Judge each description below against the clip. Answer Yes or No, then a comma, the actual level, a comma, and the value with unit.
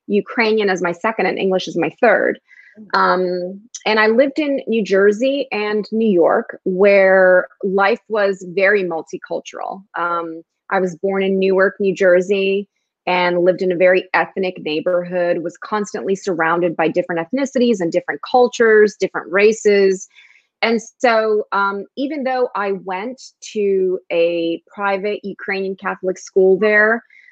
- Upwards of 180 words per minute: No, average, 140 wpm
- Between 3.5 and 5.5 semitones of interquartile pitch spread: No, average, 2.9 semitones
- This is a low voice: No, high, 195 Hz